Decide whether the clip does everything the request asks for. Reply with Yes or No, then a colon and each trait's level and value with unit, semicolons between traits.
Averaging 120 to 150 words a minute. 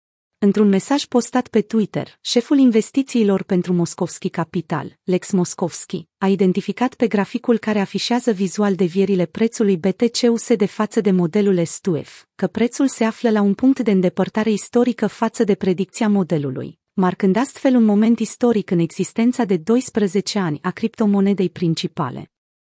Yes: average, 145 wpm